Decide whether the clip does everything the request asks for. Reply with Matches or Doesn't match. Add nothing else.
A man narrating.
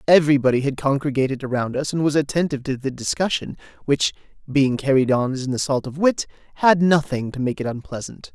Matches